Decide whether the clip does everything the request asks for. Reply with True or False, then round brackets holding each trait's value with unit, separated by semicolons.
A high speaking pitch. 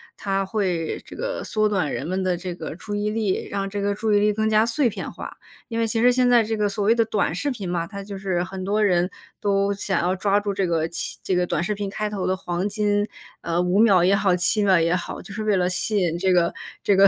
True (200 Hz)